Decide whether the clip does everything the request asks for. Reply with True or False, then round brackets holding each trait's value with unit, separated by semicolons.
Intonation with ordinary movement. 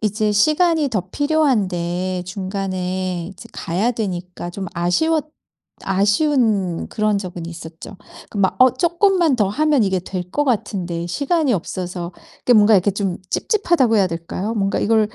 False (5.9 semitones)